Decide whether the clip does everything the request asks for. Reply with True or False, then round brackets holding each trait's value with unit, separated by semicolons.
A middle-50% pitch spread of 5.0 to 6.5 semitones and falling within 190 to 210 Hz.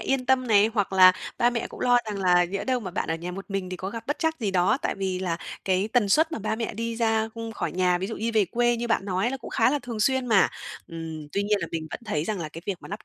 False (4.3 semitones; 205 Hz)